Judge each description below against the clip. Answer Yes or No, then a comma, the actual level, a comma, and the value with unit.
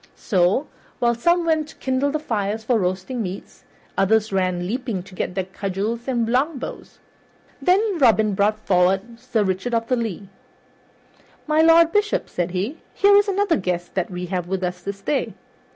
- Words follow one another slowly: No, average, 170 wpm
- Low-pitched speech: No, high, 220 Hz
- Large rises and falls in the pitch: Yes, wide, 6.5 semitones